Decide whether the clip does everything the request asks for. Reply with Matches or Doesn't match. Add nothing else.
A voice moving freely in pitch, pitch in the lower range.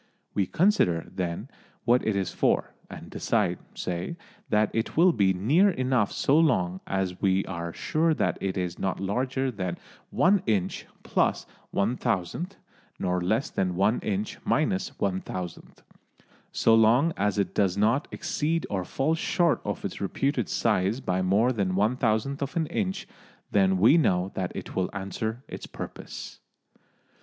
Matches